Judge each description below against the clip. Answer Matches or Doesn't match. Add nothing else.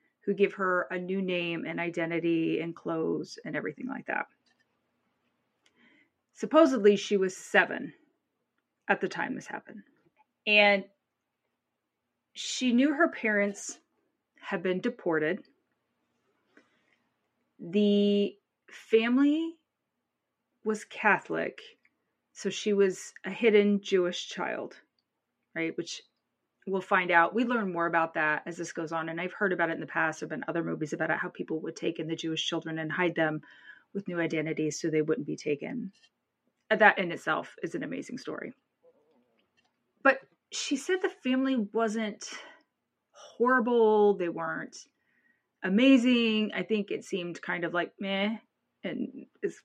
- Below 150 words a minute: Matches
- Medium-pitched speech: Doesn't match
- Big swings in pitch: Matches